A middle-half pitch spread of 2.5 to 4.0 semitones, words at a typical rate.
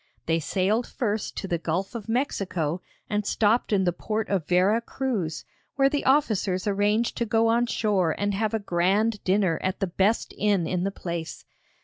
Yes: average, 3.5 semitones; average, 185 wpm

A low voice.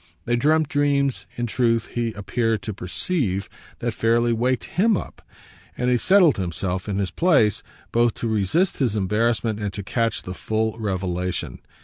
Yes: low, 115 Hz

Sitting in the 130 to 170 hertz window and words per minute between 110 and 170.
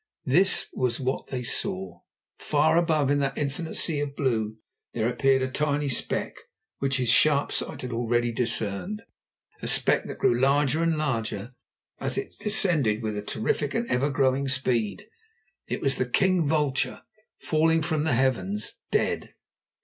Yes: low, 135 Hz; average, 155 wpm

